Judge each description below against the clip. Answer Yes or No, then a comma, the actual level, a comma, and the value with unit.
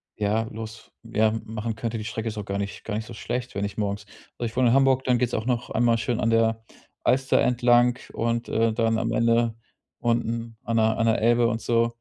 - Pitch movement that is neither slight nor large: No, narrow, 1.3 semitones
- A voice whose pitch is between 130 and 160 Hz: No, low, 115 Hz